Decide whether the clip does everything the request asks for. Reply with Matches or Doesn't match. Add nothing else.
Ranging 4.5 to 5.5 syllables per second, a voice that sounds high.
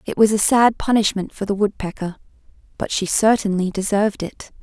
Matches